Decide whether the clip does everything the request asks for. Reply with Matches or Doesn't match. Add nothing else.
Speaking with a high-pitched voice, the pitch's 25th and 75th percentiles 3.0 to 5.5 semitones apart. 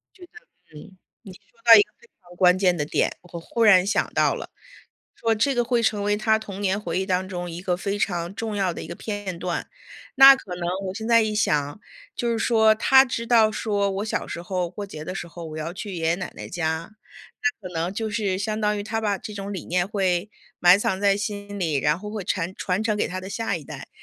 Matches